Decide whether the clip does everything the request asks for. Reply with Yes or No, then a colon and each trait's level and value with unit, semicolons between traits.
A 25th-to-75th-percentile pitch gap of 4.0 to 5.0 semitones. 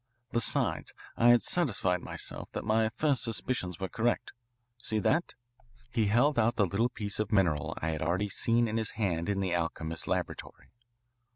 Yes: average, 4.5 semitones